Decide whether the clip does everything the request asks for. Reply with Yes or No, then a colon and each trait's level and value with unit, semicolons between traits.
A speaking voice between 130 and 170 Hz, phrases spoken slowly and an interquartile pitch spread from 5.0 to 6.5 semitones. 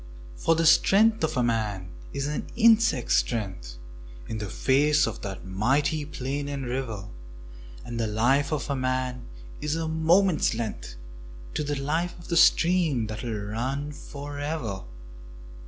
No: medium, 140 Hz; average, 150 wpm; wide, 5.6 semitones